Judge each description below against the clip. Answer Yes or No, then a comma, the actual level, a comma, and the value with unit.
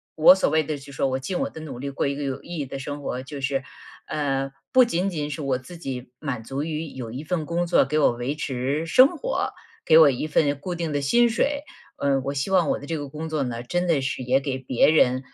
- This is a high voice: No, medium, 145 Hz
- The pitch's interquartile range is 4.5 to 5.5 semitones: No, average, 3.3 semitones